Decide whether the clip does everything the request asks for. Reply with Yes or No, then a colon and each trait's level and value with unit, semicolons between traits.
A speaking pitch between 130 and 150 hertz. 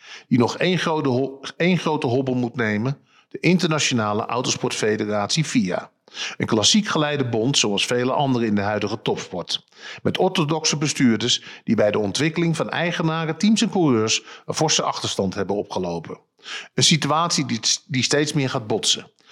Yes: medium, 140 Hz